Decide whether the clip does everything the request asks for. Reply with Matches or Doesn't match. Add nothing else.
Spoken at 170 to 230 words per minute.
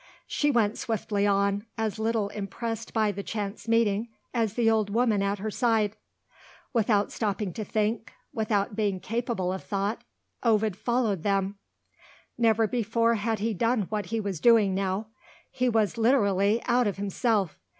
Doesn't match